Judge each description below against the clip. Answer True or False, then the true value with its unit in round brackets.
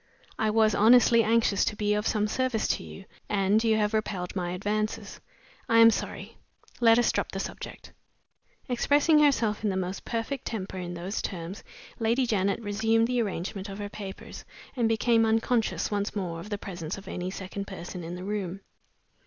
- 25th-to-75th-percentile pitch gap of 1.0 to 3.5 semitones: True (2.9 semitones)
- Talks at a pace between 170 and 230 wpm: True (180 wpm)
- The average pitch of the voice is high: True (210 Hz)